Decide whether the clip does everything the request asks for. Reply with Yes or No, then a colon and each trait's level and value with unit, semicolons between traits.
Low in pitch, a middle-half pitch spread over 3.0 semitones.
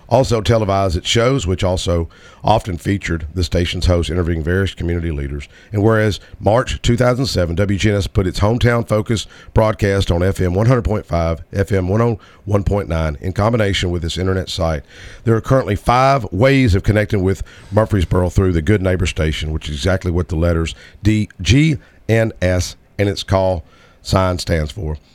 Yes: very low, 95 Hz; average, 3.6 semitones